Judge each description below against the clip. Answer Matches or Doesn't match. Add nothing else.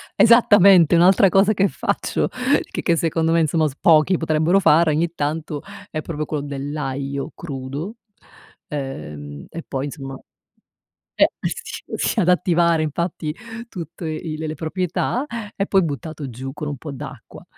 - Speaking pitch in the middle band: Matches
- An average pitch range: Matches